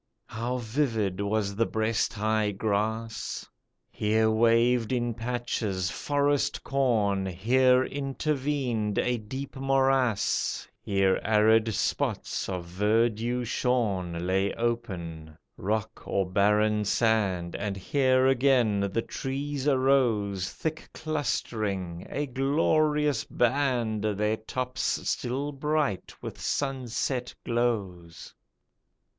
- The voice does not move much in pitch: No, average, 4.3 semitones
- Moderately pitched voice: No, low, 115 Hz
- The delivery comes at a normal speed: No, slow, 100 wpm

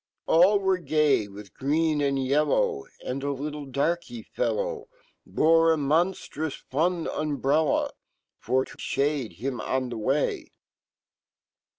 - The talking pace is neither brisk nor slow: No, slow, 110 wpm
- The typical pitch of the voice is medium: Yes, medium, 150 Hz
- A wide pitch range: No, average, 3.7 semitones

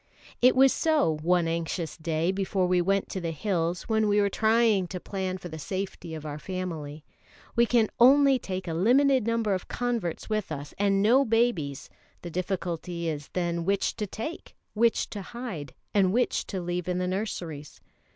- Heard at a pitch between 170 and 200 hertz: Yes, medium, 185 Hz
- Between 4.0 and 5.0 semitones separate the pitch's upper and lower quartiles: Yes, average, 4.6 semitones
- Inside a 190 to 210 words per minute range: No, average, 180 wpm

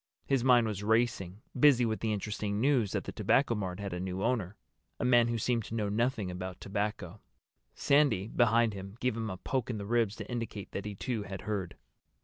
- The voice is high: No, low, 110 Hz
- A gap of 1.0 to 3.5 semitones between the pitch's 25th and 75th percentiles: Yes, average, 3.2 semitones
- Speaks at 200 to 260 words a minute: Yes, fast, 205 wpm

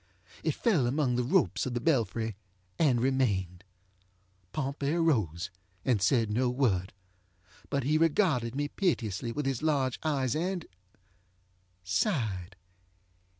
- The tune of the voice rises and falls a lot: Yes, wide, 7.2 semitones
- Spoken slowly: Yes, slow, 115 wpm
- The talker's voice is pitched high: No, low, 125 Hz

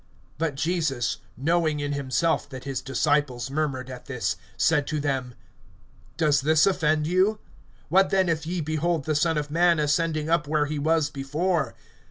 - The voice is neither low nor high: Yes, medium, 150 Hz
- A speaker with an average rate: Yes, average, 165 wpm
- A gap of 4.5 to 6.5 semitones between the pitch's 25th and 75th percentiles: No, average, 2.8 semitones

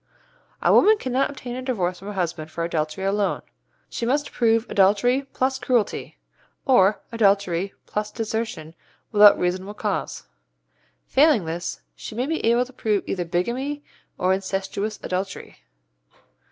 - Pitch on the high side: Yes, high, 210 Hz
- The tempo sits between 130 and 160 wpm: Yes, average, 140 wpm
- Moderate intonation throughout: Yes, average, 4.9 semitones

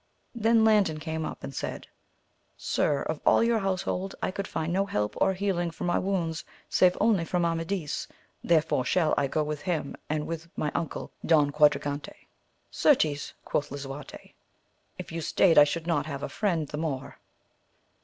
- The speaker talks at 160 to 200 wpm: Yes, average, 170 wpm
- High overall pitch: No, medium, 165 Hz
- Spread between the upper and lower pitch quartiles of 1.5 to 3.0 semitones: No, average, 3.9 semitones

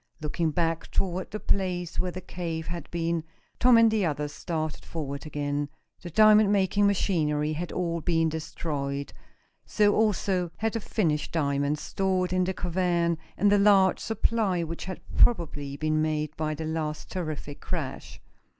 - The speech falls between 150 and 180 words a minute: Yes, average, 160 wpm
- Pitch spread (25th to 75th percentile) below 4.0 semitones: Yes, average, 3.6 semitones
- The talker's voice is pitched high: No, medium, 170 Hz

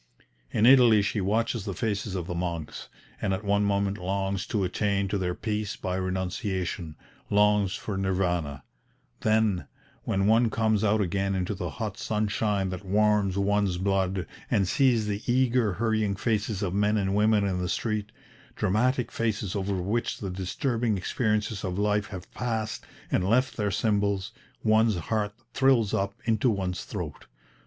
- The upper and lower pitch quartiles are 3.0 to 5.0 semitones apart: No, narrow, 2.4 semitones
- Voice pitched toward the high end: No, low, 100 Hz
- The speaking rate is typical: Yes, average, 160 wpm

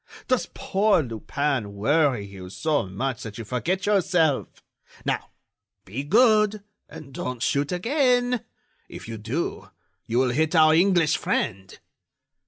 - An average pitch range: No, wide, 8.6 semitones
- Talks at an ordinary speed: No, slow, 130 wpm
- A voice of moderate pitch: Yes, medium, 150 Hz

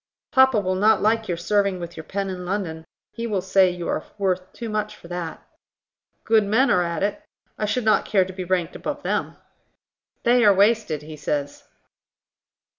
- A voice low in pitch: No, high, 190 Hz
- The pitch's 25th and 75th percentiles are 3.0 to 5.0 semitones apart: Yes, average, 3.4 semitones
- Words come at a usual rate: Yes, average, 190 wpm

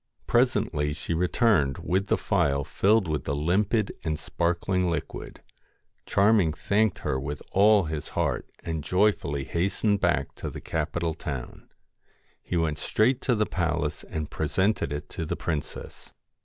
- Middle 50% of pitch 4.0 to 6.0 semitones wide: Yes, average, 5.1 semitones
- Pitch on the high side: No, very low, 85 Hz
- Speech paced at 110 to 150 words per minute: Yes, average, 145 wpm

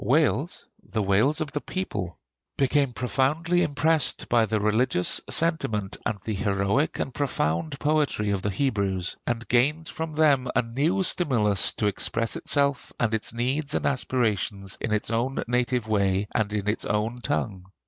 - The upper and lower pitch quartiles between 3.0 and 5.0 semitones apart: No, wide, 5.5 semitones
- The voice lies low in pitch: Yes, low, 120 Hz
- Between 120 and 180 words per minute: Yes, average, 160 wpm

